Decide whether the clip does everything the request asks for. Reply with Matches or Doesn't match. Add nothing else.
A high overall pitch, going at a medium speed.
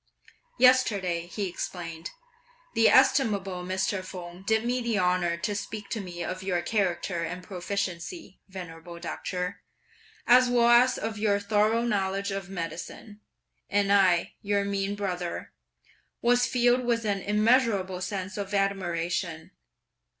Doesn't match